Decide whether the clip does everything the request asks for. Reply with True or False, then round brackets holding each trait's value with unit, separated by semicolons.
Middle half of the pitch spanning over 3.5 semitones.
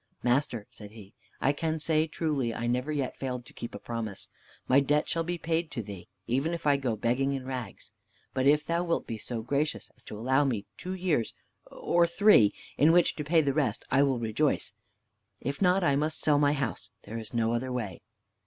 True (4.7 semitones)